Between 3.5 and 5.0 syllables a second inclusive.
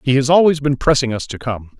No: 5.9 syllables/s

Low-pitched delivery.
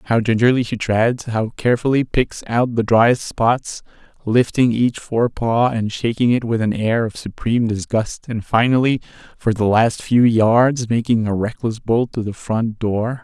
Yes: low, 115 Hz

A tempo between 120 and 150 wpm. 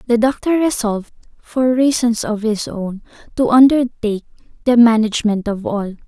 Yes: average, 140 wpm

